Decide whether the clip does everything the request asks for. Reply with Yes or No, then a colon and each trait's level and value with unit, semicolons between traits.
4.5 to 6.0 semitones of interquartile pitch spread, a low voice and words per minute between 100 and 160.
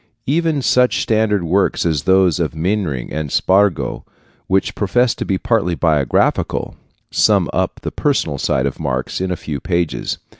Yes: average, 5.1 semitones; very low, 95 Hz; average, 155 wpm